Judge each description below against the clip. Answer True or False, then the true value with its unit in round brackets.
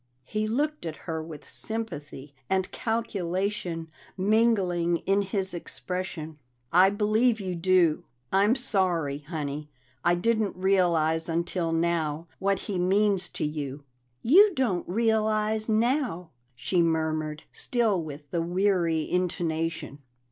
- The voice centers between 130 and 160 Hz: False (180 Hz)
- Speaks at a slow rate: True (120 wpm)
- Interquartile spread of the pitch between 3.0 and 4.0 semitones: False (4.7 semitones)